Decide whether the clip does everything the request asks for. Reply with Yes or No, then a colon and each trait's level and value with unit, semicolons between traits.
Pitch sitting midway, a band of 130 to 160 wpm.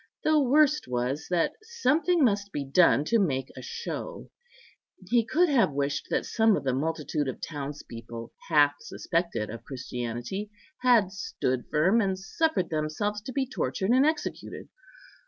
Yes: medium, 180 Hz; average, 150 wpm